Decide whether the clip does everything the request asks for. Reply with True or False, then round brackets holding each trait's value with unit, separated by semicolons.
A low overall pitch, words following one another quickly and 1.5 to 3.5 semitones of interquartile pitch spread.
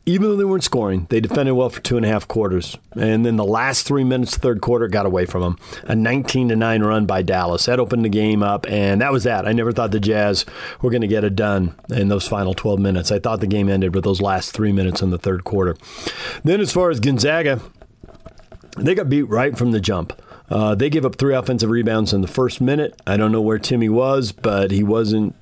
False (110 Hz; 250 wpm; 3.9 semitones)